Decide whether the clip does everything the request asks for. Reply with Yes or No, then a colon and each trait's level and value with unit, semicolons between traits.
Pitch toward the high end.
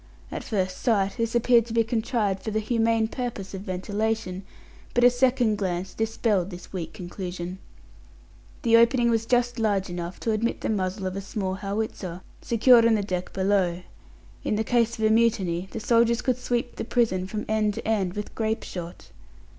Yes: high, 215 Hz